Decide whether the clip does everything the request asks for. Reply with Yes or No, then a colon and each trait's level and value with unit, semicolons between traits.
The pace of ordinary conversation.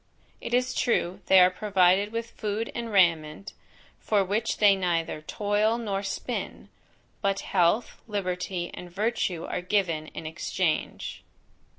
No: slow, 130 wpm